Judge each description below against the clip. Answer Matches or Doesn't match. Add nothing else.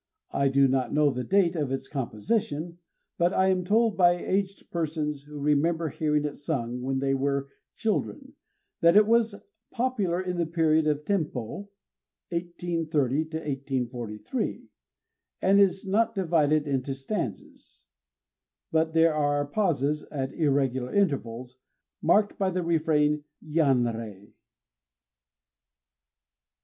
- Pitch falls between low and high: Matches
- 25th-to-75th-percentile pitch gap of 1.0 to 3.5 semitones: Doesn't match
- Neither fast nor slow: Doesn't match